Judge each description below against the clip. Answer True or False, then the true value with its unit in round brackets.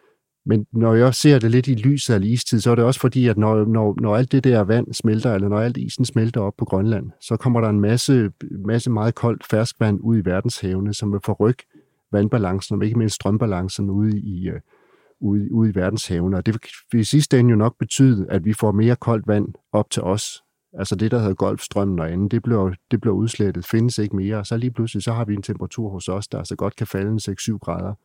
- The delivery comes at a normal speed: False (235 wpm)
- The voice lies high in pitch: False (110 Hz)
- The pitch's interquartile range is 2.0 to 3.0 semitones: True (2.7 semitones)